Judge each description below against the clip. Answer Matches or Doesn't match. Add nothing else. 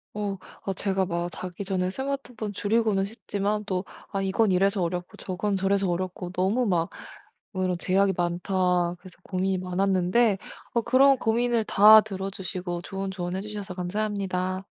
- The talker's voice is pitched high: Matches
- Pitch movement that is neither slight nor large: Doesn't match